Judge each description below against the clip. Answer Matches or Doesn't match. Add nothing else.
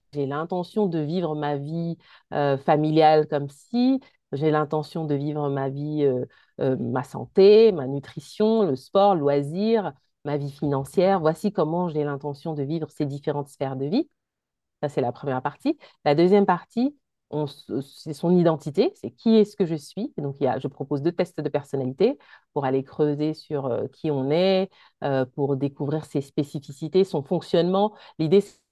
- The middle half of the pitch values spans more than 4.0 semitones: Matches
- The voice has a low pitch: Doesn't match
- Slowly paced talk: Doesn't match